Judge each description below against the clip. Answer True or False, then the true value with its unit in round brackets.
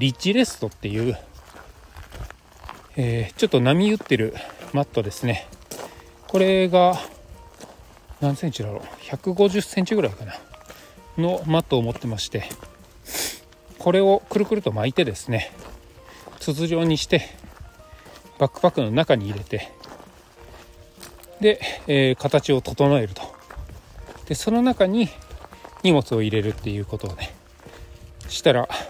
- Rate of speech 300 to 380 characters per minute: False (245 characters per minute)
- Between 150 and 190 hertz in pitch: False (130 Hz)